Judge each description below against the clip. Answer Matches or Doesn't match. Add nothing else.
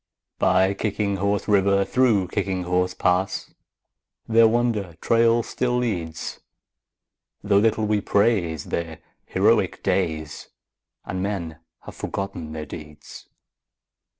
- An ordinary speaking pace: Doesn't match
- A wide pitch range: Doesn't match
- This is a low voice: Matches